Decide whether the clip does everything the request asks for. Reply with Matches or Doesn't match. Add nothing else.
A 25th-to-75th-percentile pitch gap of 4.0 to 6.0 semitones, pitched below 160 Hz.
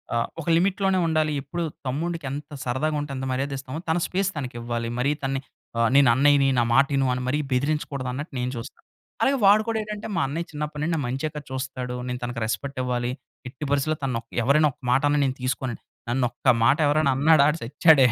Doesn't match